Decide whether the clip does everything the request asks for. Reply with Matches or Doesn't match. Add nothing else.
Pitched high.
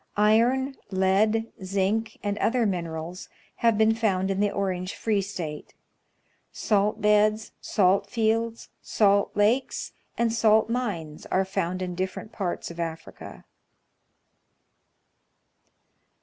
Matches